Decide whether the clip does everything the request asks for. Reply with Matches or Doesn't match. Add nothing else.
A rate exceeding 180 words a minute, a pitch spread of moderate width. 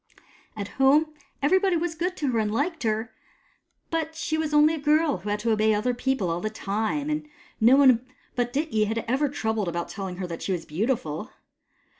Doesn't match